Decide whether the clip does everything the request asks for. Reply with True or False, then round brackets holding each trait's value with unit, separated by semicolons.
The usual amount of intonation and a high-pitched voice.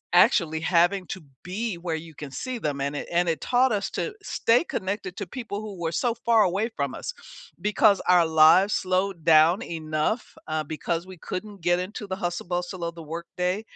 False (3.8 semitones; 180 Hz)